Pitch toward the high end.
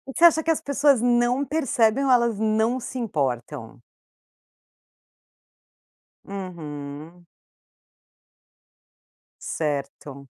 Yes: high, 220 Hz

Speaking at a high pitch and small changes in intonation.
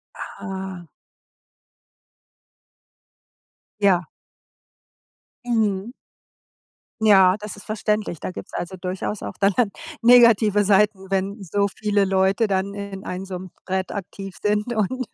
Yes: high, 200 Hz; narrow, 1.8 semitones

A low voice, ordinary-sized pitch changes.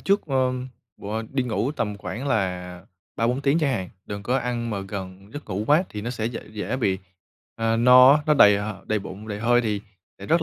Yes: low, 115 Hz; average, 4.0 semitones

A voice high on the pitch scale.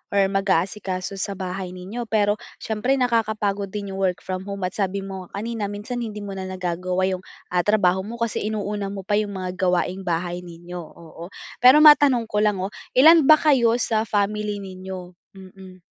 Yes: high, 195 Hz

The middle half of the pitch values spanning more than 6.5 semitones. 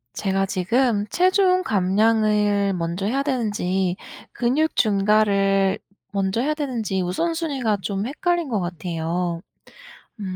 No: average, 5.2 semitones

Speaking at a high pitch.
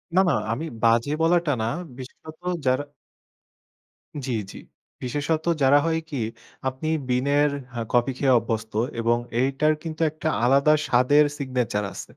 No: low, 135 Hz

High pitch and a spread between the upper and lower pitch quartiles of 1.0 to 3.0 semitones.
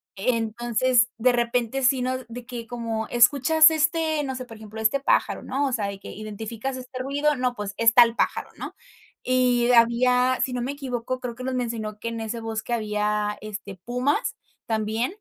Yes: high, 240 Hz; narrow, 2.5 semitones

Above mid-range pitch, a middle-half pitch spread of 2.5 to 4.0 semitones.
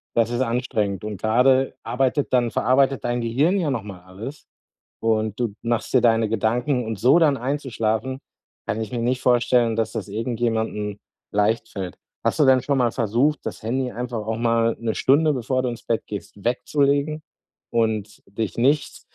No: low, 120 Hz; average, 2.9 semitones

